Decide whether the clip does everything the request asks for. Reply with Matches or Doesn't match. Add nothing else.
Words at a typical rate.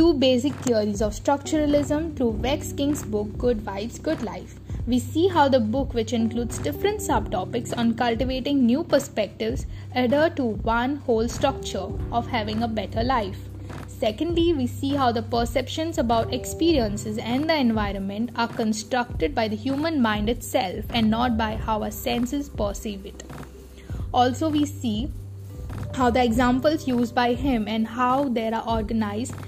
Matches